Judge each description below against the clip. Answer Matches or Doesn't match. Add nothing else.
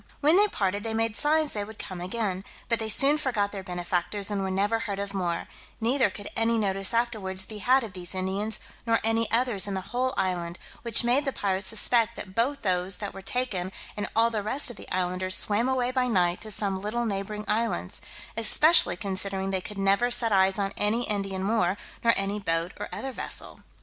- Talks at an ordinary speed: Doesn't match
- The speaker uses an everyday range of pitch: Matches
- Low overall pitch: Doesn't match